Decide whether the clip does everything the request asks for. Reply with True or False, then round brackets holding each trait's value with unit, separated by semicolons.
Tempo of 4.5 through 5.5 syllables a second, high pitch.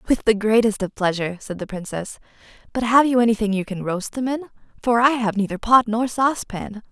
False (5.9 syllables/s; 220 Hz)